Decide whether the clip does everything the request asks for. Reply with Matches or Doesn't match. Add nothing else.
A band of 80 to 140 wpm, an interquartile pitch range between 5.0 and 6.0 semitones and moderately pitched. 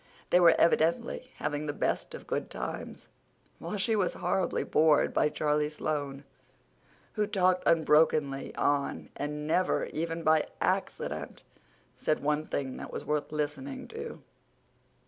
Doesn't match